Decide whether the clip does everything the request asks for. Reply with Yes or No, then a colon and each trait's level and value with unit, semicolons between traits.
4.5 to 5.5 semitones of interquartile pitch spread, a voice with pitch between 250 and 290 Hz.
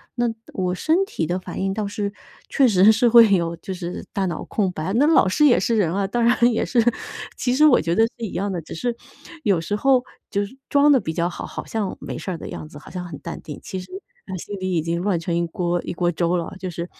No: average, 4.8 semitones; high, 190 Hz